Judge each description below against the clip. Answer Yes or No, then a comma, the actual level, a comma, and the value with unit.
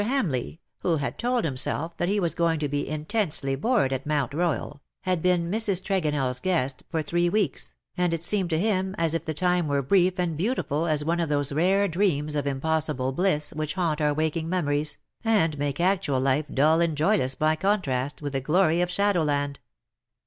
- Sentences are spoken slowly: No, average, 195 wpm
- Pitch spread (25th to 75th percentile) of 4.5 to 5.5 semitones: No, average, 3.9 semitones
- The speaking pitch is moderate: Yes, medium, 160 Hz